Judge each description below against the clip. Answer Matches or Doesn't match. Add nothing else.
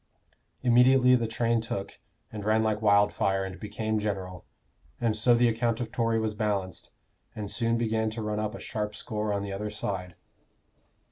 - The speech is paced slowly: Doesn't match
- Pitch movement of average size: Doesn't match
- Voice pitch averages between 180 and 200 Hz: Doesn't match